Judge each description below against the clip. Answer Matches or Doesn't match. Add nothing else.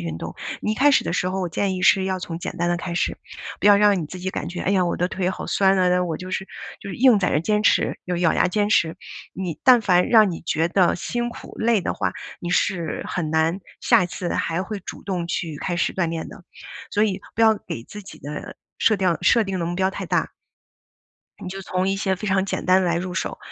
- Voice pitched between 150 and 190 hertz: Matches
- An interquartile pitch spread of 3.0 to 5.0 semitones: Doesn't match